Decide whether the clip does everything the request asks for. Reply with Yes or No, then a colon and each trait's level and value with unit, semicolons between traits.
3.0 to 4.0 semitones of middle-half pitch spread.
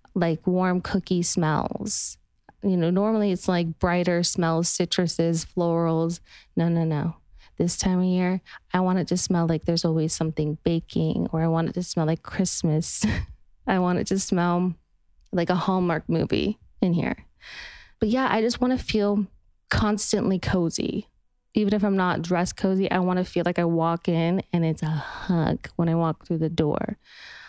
No: narrow, 2.4 semitones